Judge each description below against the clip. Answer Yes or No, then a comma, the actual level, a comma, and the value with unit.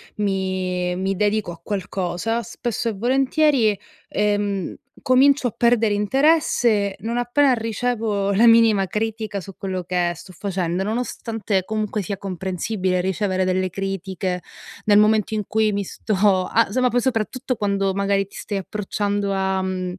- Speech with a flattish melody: No, average, 3.0 semitones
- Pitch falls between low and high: No, high, 205 Hz